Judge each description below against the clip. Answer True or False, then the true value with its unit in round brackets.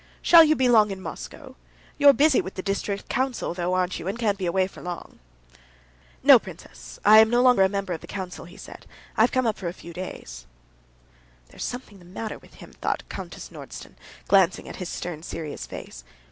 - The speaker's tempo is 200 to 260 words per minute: True (205 wpm)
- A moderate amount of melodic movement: True (4.4 semitones)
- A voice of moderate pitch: False (195 Hz)